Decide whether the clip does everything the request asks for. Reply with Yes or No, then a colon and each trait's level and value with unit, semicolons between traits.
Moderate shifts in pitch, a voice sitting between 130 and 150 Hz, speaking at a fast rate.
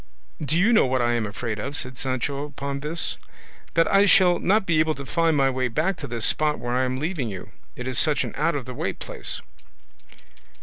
Yes: average, 4.3 semitones; medium, 140 Hz; fast, 225 wpm